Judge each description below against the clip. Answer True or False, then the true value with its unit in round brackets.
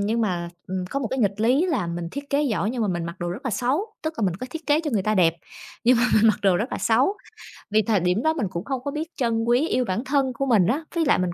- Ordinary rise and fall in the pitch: False (6.3 semitones)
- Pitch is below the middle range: False (230 Hz)